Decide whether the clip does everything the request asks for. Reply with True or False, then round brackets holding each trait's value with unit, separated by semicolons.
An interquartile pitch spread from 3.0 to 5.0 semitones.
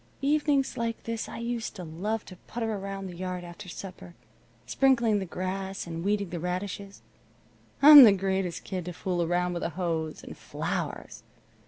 True (3.9 semitones)